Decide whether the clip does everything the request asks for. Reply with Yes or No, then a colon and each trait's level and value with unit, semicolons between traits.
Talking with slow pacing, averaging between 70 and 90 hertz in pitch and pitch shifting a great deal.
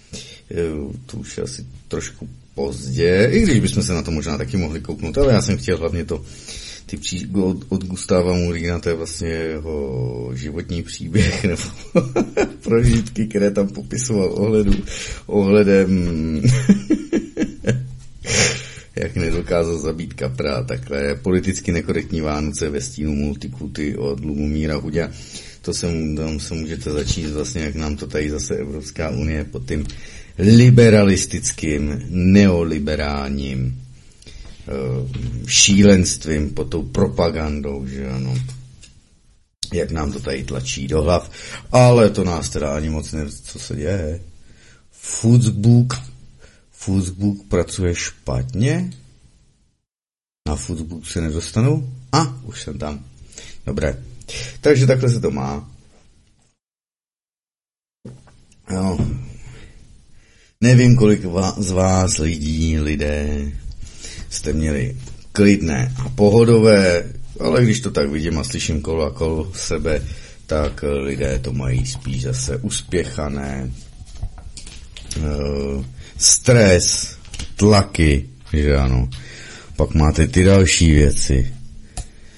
Yes: slow, 110 wpm; very low, 80 Hz; wide, 5.8 semitones